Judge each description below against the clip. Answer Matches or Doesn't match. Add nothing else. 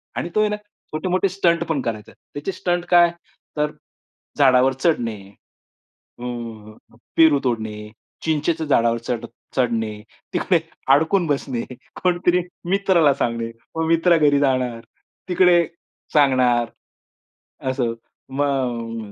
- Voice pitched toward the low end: Doesn't match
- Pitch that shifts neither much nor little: Doesn't match